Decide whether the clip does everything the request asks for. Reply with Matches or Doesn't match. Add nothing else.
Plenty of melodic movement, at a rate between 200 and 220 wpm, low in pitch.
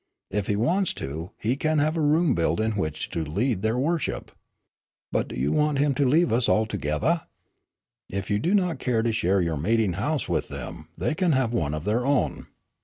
Matches